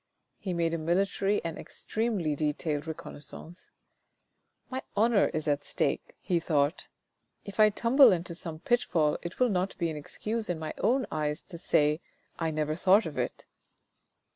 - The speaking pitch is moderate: Yes, medium, 170 Hz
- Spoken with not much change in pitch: No, average, 4.5 semitones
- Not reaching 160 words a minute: No, average, 170 wpm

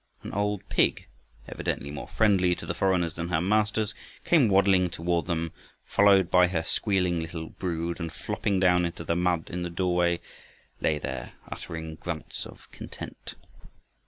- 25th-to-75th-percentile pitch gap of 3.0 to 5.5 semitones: No, narrow, 2.5 semitones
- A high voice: No, very low, 90 Hz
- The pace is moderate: Yes, average, 160 wpm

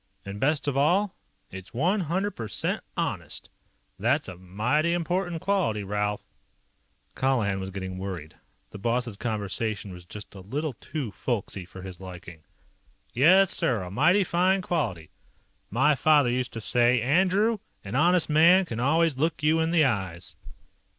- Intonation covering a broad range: Yes, wide, 8.7 semitones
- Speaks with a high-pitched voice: No, low, 125 Hz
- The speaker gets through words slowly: No, average, 150 wpm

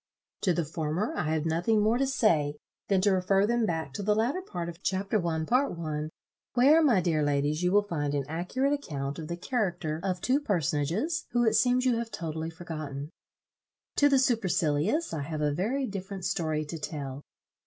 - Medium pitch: Yes, medium, 180 Hz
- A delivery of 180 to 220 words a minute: Yes, average, 195 wpm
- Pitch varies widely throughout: Yes, wide, 6.3 semitones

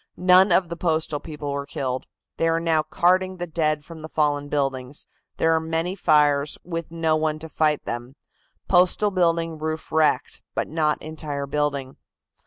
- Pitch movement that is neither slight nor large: No, narrow, 2.2 semitones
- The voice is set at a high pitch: No, medium, 155 Hz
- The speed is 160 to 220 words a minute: Yes, average, 170 wpm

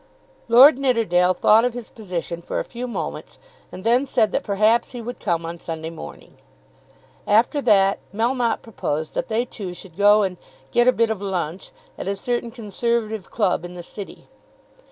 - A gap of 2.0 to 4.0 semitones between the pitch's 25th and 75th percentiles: No, average, 4.6 semitones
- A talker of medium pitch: No, high, 215 Hz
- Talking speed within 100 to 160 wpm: No, average, 175 wpm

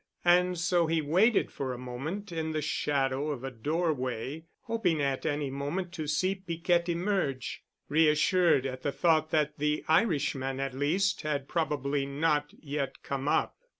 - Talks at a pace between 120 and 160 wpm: Yes, average, 155 wpm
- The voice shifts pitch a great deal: No, average, 3.7 semitones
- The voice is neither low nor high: Yes, medium, 150 Hz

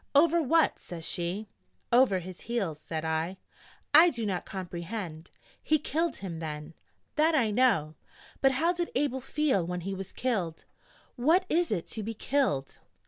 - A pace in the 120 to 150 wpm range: No, average, 160 wpm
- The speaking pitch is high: Yes, high, 215 Hz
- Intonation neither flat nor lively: No, wide, 8.7 semitones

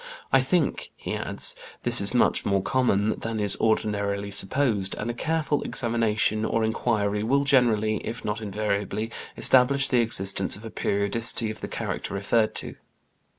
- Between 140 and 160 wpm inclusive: Yes, average, 155 wpm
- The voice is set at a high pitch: No, low, 110 Hz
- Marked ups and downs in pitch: No, average, 2.7 semitones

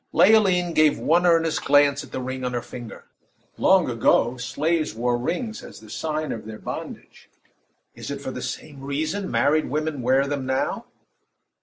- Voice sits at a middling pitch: Yes, medium, 145 Hz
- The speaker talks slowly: No, average, 170 wpm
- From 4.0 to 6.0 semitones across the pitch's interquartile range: Yes, average, 4.4 semitones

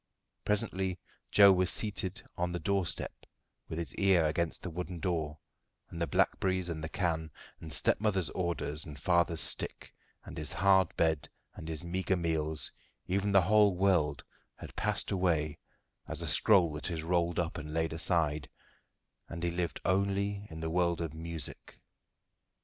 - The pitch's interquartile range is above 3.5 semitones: No, average, 2.8 semitones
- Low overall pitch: Yes, very low, 85 Hz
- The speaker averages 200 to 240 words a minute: No, average, 160 wpm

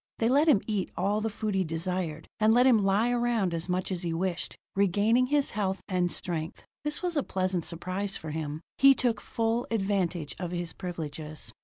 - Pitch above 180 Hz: Yes, high, 190 Hz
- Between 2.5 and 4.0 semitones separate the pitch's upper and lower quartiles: No, average, 4.6 semitones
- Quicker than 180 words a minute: Yes, average, 195 wpm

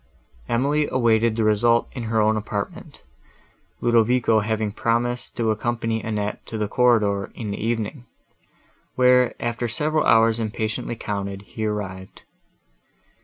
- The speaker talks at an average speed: No, slow, 125 wpm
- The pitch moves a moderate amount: No, narrow, 1.9 semitones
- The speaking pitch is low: Yes, low, 115 Hz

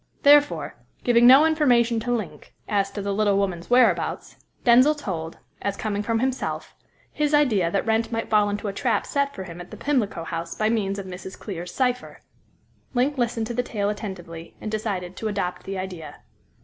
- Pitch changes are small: No, average, 4.4 semitones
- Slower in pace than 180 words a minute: No, average, 190 wpm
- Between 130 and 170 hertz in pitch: No, high, 215 Hz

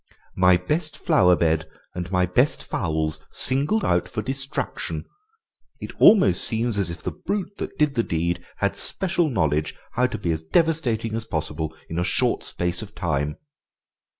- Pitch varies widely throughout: Yes, wide, 8.3 semitones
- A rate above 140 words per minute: Yes, average, 165 wpm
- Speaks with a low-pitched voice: Yes, very low, 95 Hz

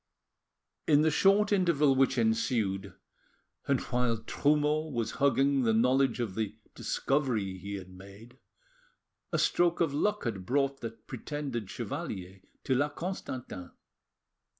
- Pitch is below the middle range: Yes, low, 130 Hz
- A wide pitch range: No, average, 5.0 semitones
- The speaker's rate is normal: No, slow, 125 wpm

